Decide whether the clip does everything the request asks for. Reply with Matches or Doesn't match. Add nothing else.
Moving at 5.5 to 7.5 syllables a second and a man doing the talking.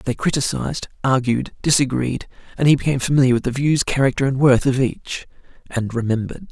Matches